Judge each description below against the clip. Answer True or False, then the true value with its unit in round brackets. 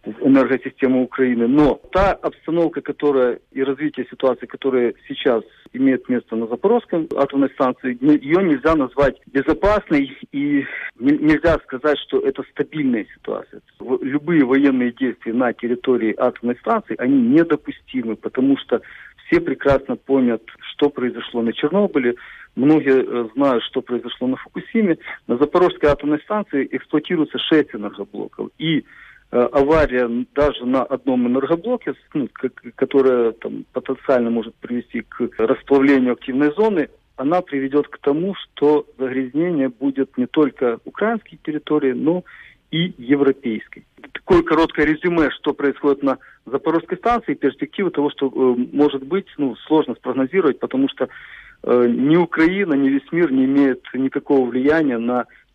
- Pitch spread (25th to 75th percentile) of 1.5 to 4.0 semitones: False (4.5 semitones)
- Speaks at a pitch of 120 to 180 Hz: True (140 Hz)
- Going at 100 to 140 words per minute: True (125 wpm)